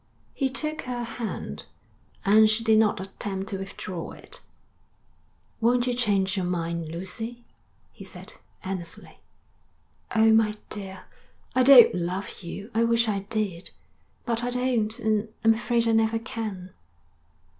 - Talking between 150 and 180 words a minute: No, average, 140 wpm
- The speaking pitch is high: Yes, high, 220 Hz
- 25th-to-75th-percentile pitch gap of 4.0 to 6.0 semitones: No, average, 3.4 semitones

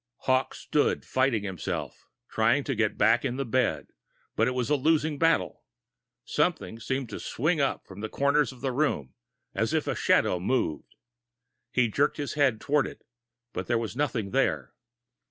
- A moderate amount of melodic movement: Yes, average, 4.0 semitones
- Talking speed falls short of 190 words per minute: Yes, average, 175 wpm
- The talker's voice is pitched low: Yes, low, 130 Hz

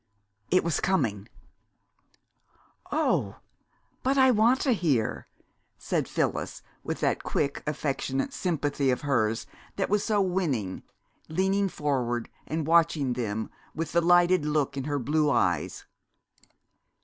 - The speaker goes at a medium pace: No, slow, 125 wpm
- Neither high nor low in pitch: Yes, medium, 150 Hz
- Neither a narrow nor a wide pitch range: No, wide, 5.7 semitones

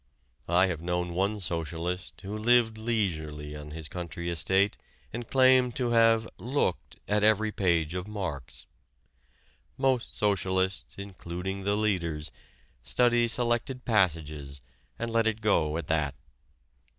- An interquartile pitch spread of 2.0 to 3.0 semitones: No, average, 5.0 semitones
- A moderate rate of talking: No, slow, 125 wpm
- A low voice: Yes, very low, 95 Hz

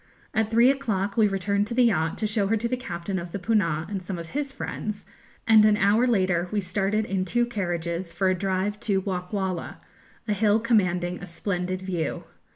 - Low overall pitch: No, high, 200 Hz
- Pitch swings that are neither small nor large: Yes, average, 3.2 semitones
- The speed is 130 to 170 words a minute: No, average, 200 wpm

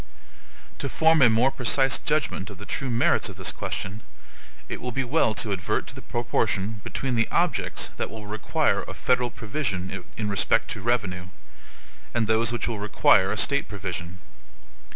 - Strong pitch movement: No, average, 3.9 semitones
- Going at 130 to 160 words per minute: No, average, 175 wpm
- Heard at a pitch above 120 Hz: No, low, 110 Hz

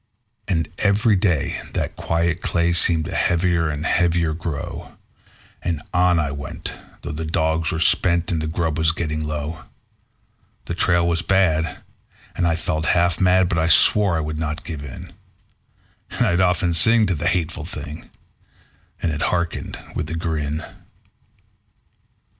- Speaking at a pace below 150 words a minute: No, average, 155 wpm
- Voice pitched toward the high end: No, very low, 85 Hz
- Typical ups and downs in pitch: No, narrow, 2.0 semitones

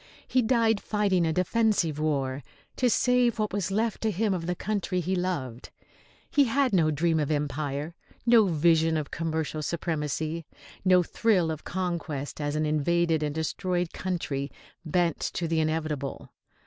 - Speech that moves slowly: No, average, 155 wpm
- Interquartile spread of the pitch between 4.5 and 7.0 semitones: No, average, 4.1 semitones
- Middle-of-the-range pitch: Yes, medium, 170 Hz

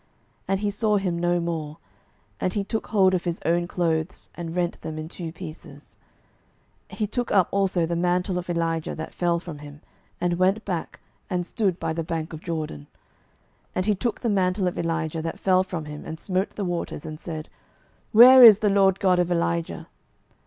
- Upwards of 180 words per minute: Yes, average, 200 wpm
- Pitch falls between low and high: Yes, medium, 175 Hz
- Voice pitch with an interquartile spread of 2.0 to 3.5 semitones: Yes, average, 2.7 semitones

